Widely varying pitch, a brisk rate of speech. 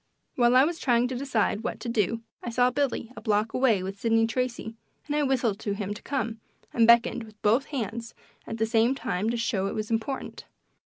No: narrow, 2.4 semitones; fast, 215 wpm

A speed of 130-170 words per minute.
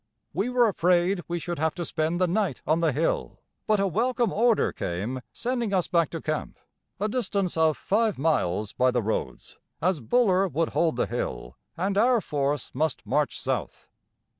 No: average, 180 wpm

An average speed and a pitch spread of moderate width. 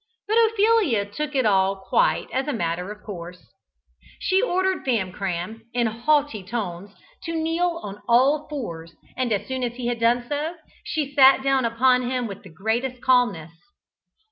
No: average, 165 wpm; wide, 6.4 semitones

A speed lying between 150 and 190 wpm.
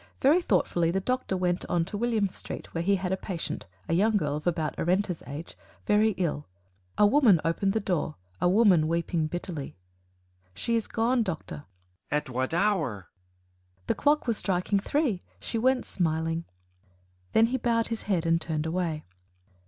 Yes: average, 170 wpm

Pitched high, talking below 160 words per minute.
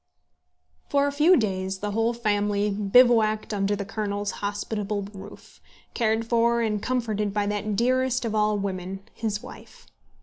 Yes: high, 210 Hz; average, 145 wpm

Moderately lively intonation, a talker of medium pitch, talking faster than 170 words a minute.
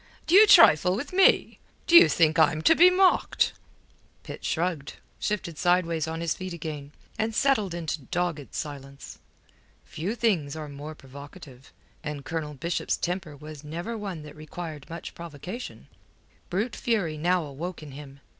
No: average, 3.8 semitones; medium, 165 Hz; average, 145 wpm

